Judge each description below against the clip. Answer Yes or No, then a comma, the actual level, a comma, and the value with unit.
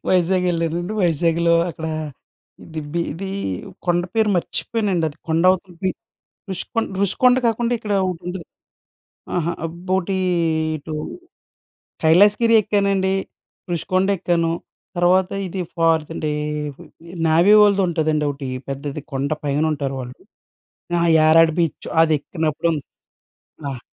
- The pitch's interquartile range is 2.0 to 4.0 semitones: Yes, average, 3.1 semitones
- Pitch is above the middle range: No, medium, 170 Hz